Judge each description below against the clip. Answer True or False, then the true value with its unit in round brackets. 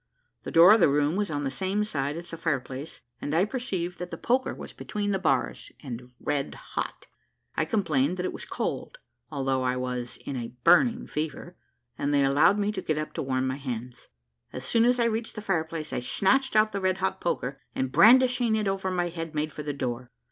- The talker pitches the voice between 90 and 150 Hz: False (165 Hz)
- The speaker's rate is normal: False (225 wpm)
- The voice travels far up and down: True (6.9 semitones)